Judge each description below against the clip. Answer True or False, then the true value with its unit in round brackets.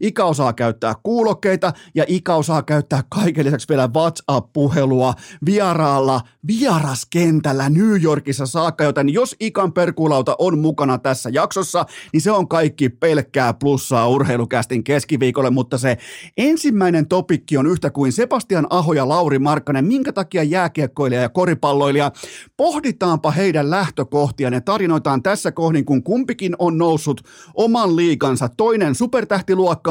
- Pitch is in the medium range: True (155 Hz)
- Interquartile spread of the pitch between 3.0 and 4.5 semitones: False (4.9 semitones)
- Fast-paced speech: False (130 wpm)